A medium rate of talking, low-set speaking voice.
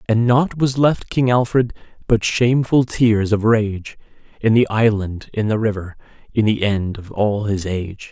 Yes: average, 175 wpm; low, 110 Hz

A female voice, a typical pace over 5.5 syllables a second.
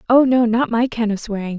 Yes: female; 5.8 syllables/s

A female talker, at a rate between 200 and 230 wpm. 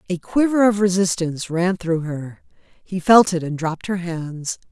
No: female; average, 180 wpm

